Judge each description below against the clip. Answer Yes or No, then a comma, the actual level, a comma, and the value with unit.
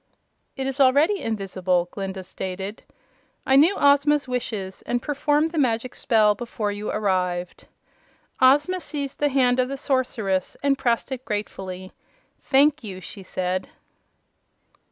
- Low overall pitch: No, high, 240 Hz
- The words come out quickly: No, slow, 135 wpm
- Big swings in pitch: Yes, wide, 6.3 semitones